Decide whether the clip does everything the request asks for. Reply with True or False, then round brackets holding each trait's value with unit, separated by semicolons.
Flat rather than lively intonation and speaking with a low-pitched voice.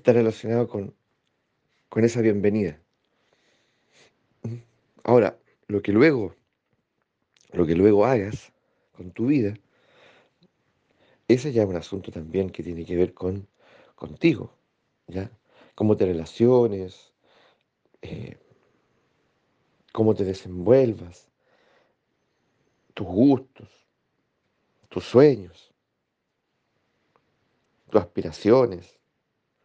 False (3.5 semitones; 105 Hz)